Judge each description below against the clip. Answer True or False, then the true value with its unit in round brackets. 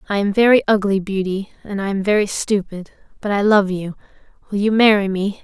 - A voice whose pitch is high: True (200 Hz)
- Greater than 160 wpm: True (200 wpm)